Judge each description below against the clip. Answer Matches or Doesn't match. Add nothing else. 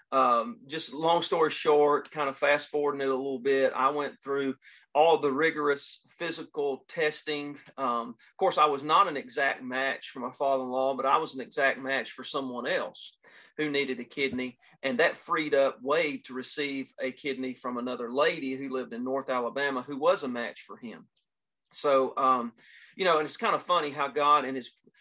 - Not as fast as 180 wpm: Doesn't match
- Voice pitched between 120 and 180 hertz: Matches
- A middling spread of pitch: Doesn't match